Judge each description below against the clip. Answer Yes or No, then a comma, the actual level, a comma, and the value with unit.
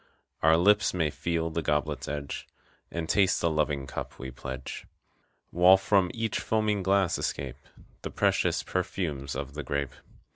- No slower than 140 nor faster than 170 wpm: Yes, average, 150 wpm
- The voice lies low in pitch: Yes, very low, 80 Hz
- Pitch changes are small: No, average, 5.0 semitones